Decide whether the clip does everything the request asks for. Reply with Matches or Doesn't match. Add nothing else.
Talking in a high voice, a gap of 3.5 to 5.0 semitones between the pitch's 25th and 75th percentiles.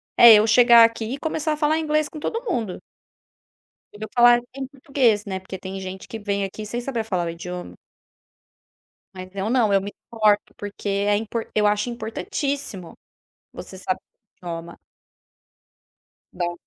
Matches